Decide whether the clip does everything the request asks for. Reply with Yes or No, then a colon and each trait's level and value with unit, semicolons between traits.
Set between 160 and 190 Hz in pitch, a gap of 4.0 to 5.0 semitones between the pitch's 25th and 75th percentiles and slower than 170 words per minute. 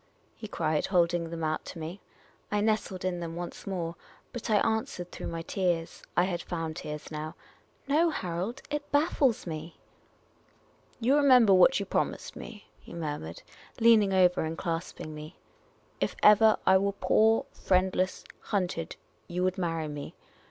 No: medium, 185 Hz; average, 4.5 semitones; average, 175 wpm